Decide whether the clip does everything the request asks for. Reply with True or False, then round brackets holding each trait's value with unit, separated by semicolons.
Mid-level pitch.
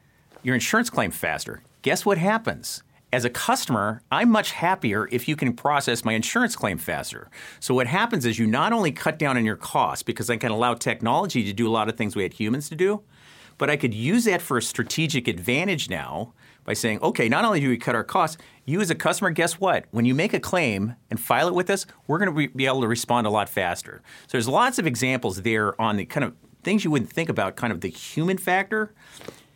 False (125 Hz)